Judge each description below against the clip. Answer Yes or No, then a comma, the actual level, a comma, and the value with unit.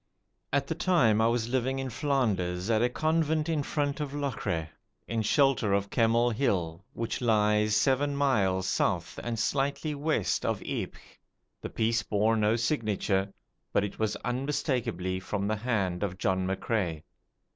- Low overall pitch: Yes, low, 115 Hz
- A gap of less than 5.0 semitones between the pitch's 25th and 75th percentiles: No, average, 5.3 semitones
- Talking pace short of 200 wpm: Yes, average, 155 wpm